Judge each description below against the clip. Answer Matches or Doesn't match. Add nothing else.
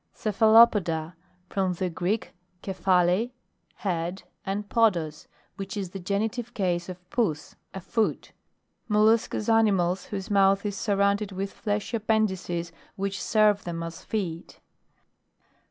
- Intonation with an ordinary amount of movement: Matches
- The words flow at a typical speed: Doesn't match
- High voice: Matches